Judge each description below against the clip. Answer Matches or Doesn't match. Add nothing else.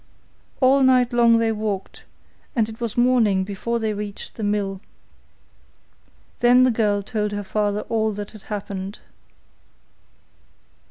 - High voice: Matches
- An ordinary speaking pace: Doesn't match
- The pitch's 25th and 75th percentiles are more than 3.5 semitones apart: Doesn't match